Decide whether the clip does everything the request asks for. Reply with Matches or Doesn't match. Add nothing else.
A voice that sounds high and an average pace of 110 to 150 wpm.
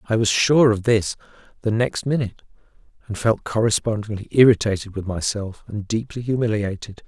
Doesn't match